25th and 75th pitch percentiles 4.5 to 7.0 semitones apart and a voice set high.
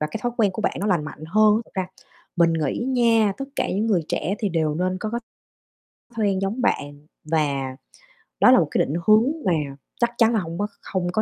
Yes: average, 5.1 semitones; high, 195 Hz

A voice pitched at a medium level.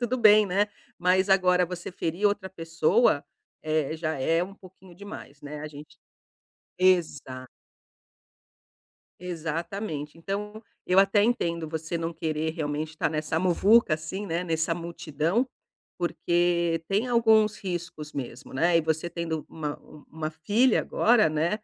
Yes: medium, 170 Hz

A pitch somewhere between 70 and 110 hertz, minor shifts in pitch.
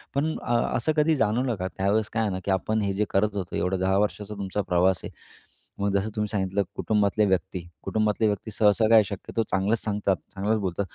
Yes: low, 105 Hz; narrow, 2.2 semitones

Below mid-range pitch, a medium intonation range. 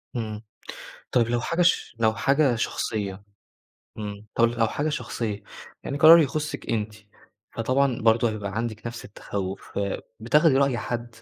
Yes: low, 115 Hz; average, 4.0 semitones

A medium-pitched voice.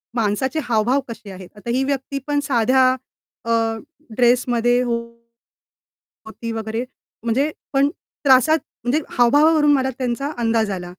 No: high, 245 Hz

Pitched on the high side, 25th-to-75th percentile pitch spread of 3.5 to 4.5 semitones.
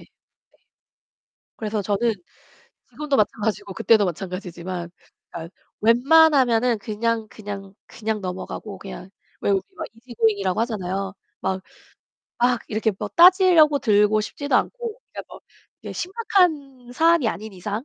No: high, 220 Hz; average, 5.2 semitones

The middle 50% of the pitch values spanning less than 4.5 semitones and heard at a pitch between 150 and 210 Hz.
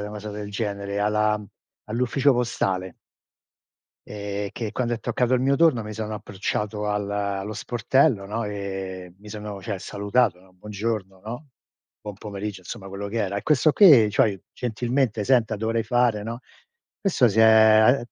No: average, 2.7 semitones; low, 105 Hz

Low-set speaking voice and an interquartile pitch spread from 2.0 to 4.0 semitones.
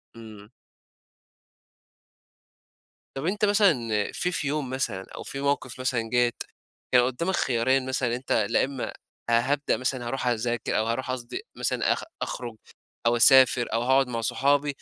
Yes: low, 130 Hz; narrow, 2.5 semitones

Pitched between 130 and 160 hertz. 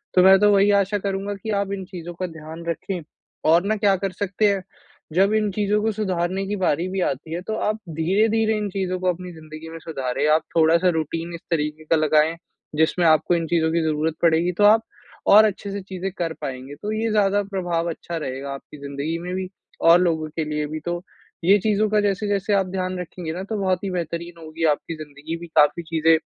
No: medium, 175 Hz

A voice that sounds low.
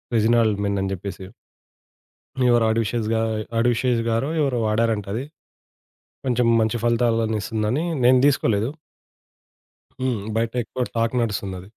Yes: low, 115 Hz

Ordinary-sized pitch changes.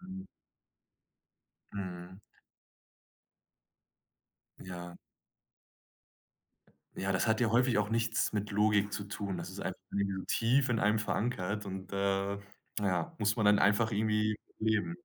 No: narrow, 2.2 semitones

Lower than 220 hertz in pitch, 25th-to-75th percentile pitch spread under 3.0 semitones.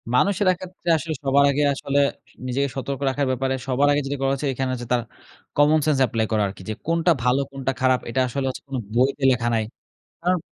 Yes: low, 135 Hz; narrow, 2.4 semitones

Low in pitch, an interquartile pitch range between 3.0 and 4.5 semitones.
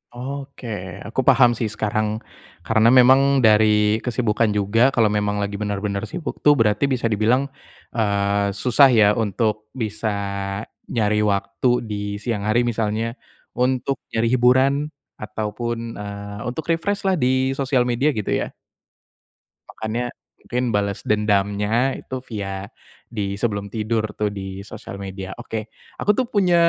Yes: low, 110 Hz; average, 3.5 semitones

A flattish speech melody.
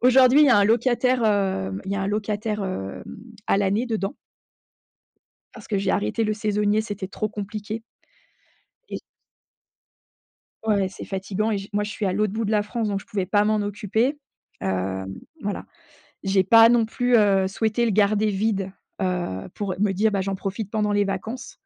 Yes: narrow, 2.2 semitones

